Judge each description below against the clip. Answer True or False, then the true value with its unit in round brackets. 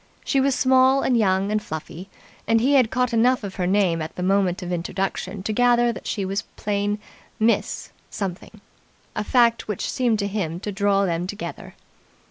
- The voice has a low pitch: False (205 Hz)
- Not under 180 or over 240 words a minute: True (185 wpm)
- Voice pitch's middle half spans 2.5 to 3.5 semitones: False (3.9 semitones)